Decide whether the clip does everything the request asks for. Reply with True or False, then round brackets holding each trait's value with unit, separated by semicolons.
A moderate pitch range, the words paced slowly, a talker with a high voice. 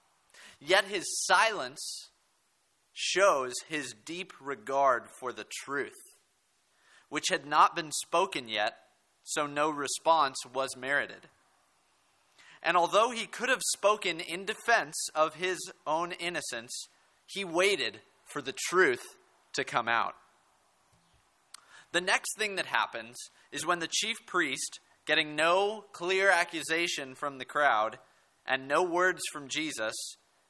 False (4.5 semitones; 125 wpm; 160 Hz)